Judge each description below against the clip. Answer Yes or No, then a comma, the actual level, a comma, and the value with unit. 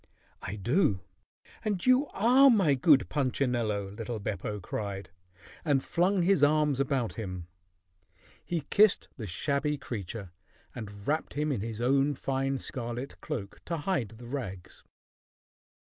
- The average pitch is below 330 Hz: Yes, low, 135 Hz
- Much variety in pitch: Yes, wide, 6.1 semitones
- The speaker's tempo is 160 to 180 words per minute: No, slow, 135 wpm